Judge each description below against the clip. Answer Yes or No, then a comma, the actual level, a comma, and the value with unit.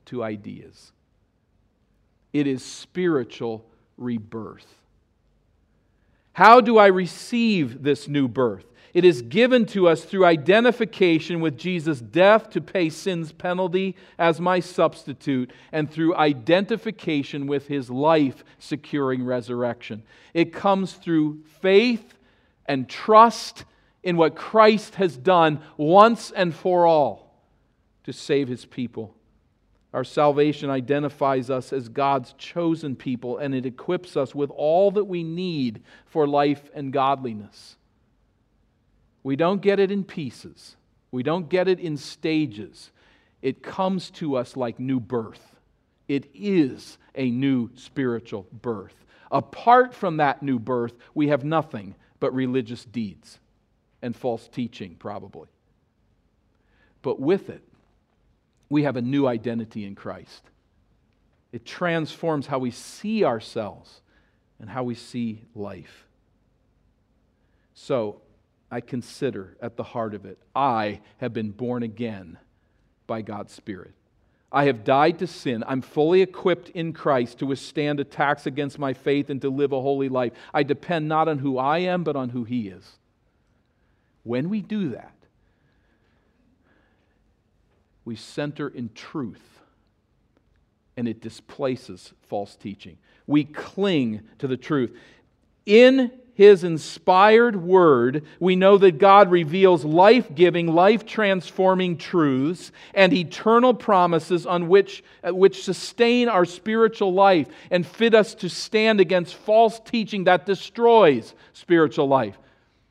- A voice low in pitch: No, medium, 145 Hz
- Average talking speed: No, slow, 130 wpm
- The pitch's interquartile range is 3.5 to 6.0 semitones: No, wide, 7.1 semitones